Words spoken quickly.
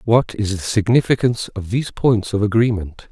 No: average, 175 wpm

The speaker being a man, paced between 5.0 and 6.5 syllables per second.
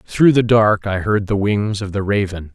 No: male; 4.5 syllables/s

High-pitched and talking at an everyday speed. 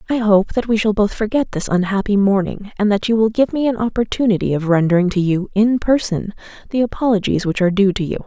No: high, 210 Hz; fast, 225 wpm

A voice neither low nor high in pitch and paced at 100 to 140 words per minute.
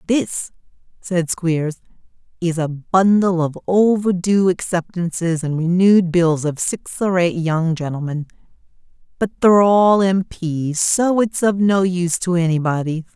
Yes: medium, 175 Hz; slow, 135 wpm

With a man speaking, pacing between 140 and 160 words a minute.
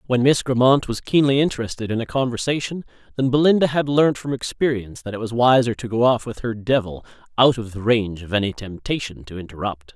No: male; fast, 205 wpm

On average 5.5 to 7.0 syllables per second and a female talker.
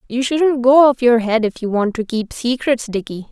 No: 4.8 syllables/s; female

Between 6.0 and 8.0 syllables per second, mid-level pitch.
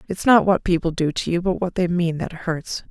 No: 5.2 syllables/s; medium, 175 Hz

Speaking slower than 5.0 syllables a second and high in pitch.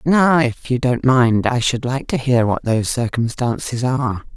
No: 4.6 syllables/s; low, 125 Hz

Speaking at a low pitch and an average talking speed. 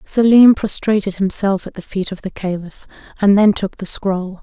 No: high, 195 Hz; average, 190 wpm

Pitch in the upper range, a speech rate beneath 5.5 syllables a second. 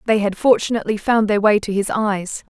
No: high, 210 Hz; 5.6 syllables/s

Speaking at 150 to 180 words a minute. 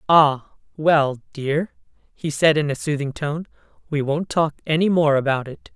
Yes: average, 165 wpm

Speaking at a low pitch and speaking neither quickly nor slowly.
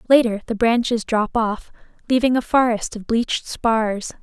No: high, 230 Hz; average, 155 wpm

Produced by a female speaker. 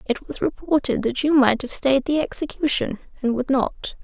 Yes: female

